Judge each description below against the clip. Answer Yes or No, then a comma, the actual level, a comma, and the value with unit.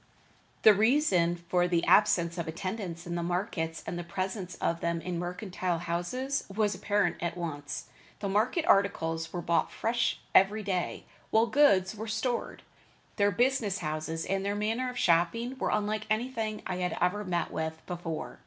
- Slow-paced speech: No, average, 165 wpm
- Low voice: No, medium, 185 Hz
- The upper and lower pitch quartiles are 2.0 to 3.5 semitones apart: No, average, 4.0 semitones